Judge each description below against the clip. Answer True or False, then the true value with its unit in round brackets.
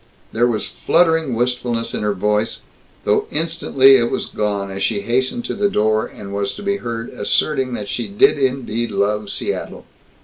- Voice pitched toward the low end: True (120 Hz)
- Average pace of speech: True (180 wpm)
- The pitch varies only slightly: False (4.5 semitones)